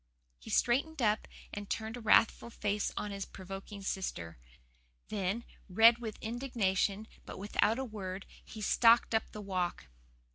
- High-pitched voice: Yes, high, 210 Hz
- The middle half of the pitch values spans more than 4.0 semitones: No, average, 3.0 semitones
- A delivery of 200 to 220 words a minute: No, average, 145 wpm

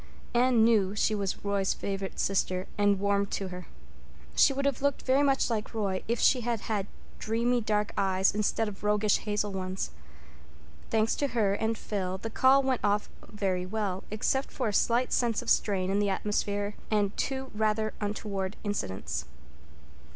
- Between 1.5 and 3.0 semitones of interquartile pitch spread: Yes, narrow, 2.6 semitones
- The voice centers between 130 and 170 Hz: No, high, 210 Hz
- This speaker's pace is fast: No, average, 175 wpm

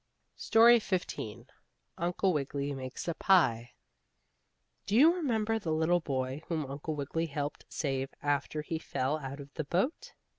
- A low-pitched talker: No, medium, 155 Hz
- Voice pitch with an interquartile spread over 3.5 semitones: Yes, average, 5.1 semitones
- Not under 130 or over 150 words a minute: Yes, average, 145 wpm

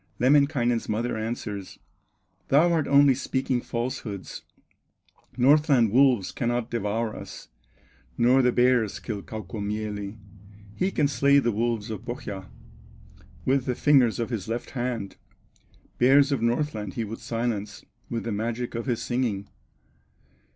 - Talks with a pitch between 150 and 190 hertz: No, low, 120 Hz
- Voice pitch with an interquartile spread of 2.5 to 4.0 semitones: Yes, average, 3.2 semitones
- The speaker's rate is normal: No, slow, 130 wpm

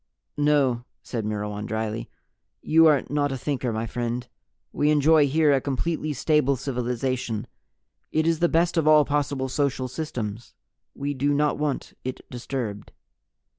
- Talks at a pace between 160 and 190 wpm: No, average, 145 wpm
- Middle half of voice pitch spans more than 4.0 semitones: No, average, 3.7 semitones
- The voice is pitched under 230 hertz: Yes, low, 135 Hz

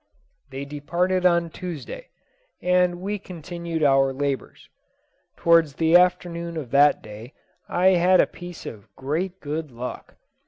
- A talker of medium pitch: Yes, medium, 170 Hz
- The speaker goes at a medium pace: No, slow, 130 wpm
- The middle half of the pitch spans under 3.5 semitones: No, average, 4.1 semitones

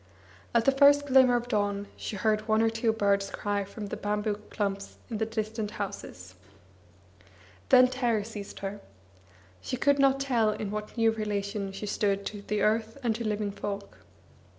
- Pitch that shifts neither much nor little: No, narrow, 2.2 semitones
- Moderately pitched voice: No, high, 215 Hz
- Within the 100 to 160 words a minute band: No, average, 175 wpm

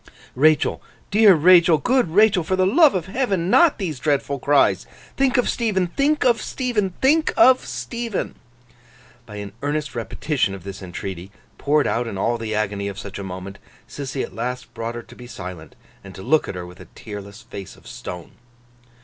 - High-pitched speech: No, medium, 140 Hz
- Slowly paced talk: No, average, 185 wpm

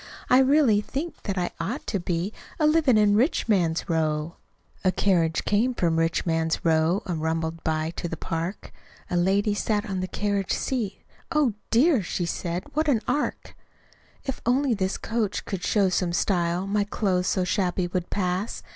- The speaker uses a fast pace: No, average, 175 wpm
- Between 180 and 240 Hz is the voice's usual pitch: Yes, high, 190 Hz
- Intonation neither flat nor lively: Yes, average, 4.5 semitones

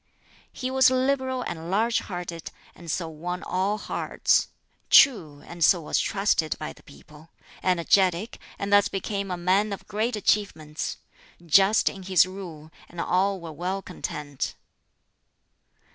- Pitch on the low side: No, medium, 185 Hz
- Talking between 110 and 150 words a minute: Yes, average, 140 wpm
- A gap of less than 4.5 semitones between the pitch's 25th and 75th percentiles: Yes, average, 3.4 semitones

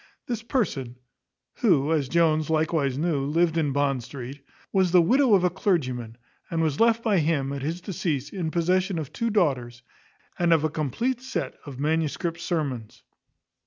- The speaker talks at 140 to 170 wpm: Yes, average, 165 wpm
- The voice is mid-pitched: Yes, medium, 160 Hz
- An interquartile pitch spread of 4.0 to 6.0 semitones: Yes, average, 4.5 semitones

